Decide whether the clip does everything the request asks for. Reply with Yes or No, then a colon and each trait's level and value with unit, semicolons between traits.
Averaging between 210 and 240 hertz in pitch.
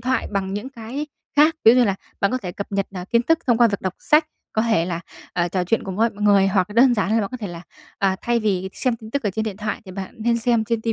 Yes: high, 215 Hz